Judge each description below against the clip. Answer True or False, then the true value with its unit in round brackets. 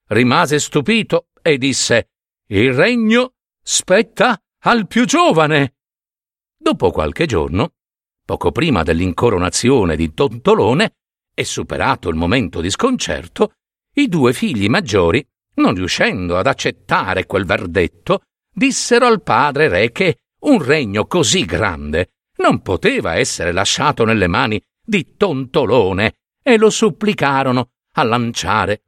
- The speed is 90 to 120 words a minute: True (115 wpm)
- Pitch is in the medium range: True (155 Hz)